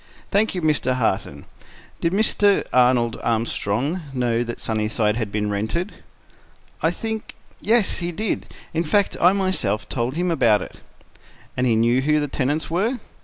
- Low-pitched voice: Yes, low, 130 Hz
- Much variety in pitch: Yes, wide, 7.7 semitones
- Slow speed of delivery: No, average, 150 wpm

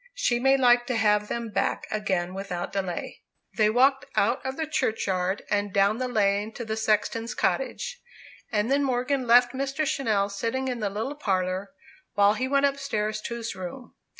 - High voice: Yes, high, 225 Hz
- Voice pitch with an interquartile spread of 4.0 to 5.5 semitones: Yes, average, 4.3 semitones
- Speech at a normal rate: Yes, average, 175 wpm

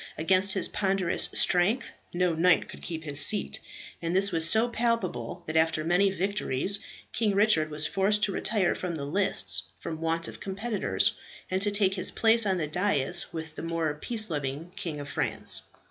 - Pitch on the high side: No, medium, 180 Hz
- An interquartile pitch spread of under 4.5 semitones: Yes, average, 4.1 semitones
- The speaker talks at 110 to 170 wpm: No, average, 180 wpm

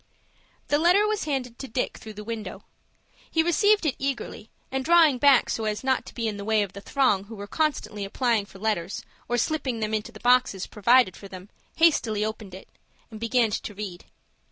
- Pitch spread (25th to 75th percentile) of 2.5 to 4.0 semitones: No, average, 4.7 semitones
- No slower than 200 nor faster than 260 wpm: Yes, fast, 205 wpm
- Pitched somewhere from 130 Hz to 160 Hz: No, high, 230 Hz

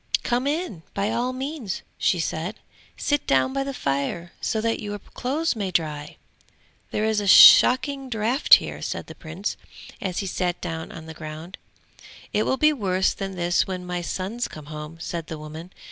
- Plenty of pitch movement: Yes, wide, 6.7 semitones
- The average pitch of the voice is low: No, high, 190 Hz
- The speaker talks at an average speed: Yes, average, 180 wpm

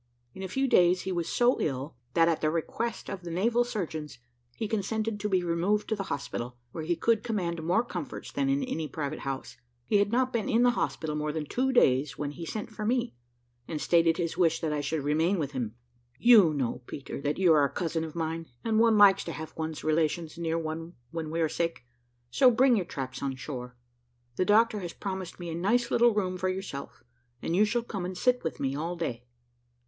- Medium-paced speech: No, fast, 225 wpm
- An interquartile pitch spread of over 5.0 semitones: Yes, wide, 5.4 semitones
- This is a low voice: No, medium, 170 Hz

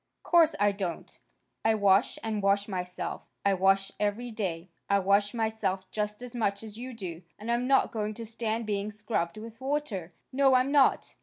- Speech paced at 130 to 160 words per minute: No, average, 180 wpm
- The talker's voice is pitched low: No, high, 210 Hz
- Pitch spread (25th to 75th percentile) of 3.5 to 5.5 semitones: No, average, 2.9 semitones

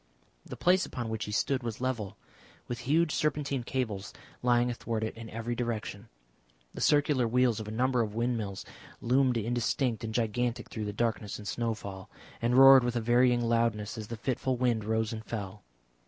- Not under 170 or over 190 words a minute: Yes, average, 180 wpm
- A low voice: Yes, low, 120 Hz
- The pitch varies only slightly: Yes, narrow, 2.2 semitones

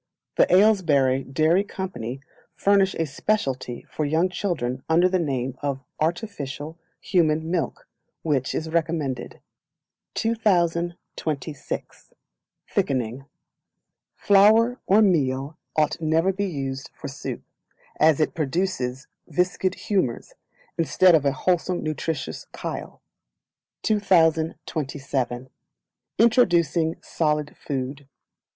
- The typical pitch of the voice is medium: Yes, medium, 160 Hz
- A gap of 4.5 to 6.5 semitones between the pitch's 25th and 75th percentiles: Yes, average, 5.1 semitones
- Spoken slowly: Yes, slow, 100 wpm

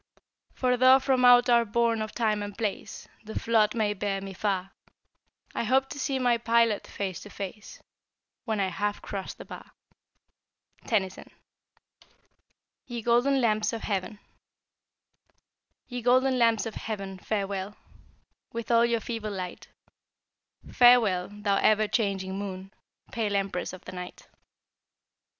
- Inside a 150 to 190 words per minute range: No, slow, 135 wpm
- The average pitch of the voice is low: No, high, 215 Hz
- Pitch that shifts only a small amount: No, average, 3.1 semitones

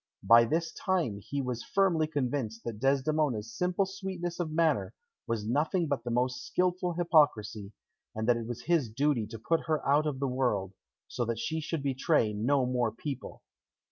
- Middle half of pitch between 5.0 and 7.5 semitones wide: Yes, wide, 5.6 semitones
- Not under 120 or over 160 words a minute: No, average, 175 wpm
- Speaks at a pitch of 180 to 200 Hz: No, low, 135 Hz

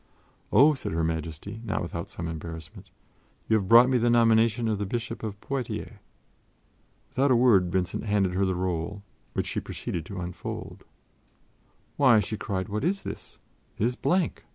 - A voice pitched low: Yes, low, 105 Hz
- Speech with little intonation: No, average, 4.9 semitones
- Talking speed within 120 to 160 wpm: No, average, 170 wpm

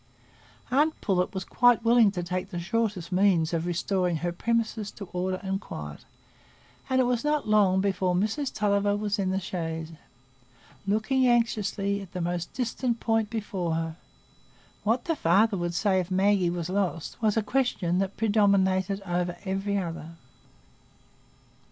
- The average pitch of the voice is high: Yes, high, 195 Hz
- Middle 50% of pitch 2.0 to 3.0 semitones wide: No, average, 3.6 semitones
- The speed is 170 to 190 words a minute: No, average, 155 wpm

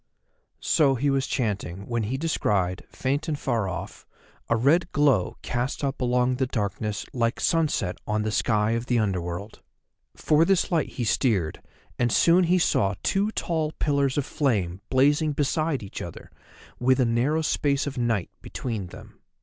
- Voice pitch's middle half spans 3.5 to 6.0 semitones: Yes, wide, 5.4 semitones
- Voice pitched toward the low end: Yes, low, 125 Hz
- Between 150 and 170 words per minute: Yes, average, 165 wpm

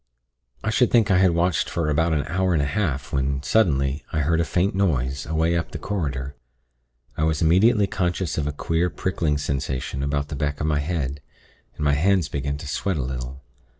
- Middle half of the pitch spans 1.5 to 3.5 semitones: No, average, 3.9 semitones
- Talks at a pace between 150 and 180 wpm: No, fast, 205 wpm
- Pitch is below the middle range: Yes, very low, 75 Hz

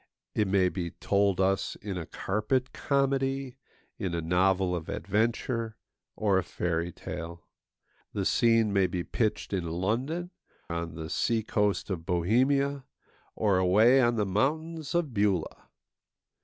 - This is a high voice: No, low, 105 Hz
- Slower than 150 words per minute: Yes, average, 140 wpm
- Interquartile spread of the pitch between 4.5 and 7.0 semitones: Yes, wide, 5.5 semitones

